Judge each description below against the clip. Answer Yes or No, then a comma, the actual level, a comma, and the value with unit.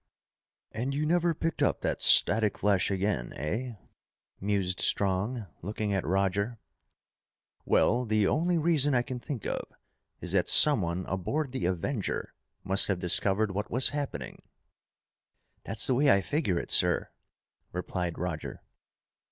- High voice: No, low, 105 Hz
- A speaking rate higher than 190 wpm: No, slow, 135 wpm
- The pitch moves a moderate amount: No, wide, 5.8 semitones